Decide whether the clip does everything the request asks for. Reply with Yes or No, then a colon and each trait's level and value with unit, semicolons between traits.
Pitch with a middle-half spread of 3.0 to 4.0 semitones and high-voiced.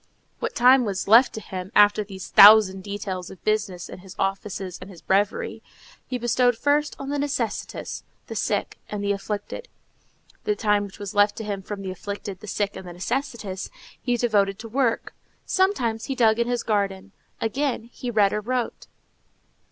Yes: average, 3.6 semitones; high, 210 Hz